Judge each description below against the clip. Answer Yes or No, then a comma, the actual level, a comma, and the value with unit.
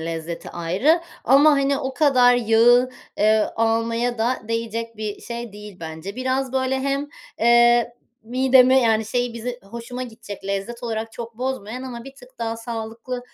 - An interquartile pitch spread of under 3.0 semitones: Yes, narrow, 2.4 semitones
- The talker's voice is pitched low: No, high, 235 Hz